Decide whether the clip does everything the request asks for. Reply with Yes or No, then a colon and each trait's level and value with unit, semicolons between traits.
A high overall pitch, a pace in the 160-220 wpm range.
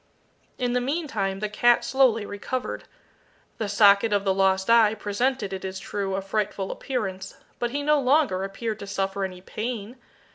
Yes: high, 210 Hz; average, 170 wpm